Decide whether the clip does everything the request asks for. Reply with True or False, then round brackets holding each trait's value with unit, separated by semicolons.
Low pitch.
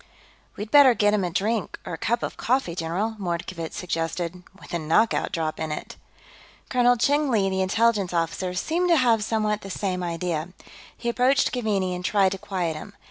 False (195 Hz)